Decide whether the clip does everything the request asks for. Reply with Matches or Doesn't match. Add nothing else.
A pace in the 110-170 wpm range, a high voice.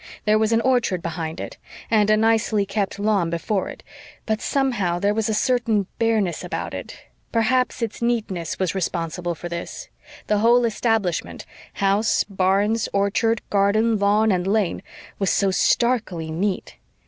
Matches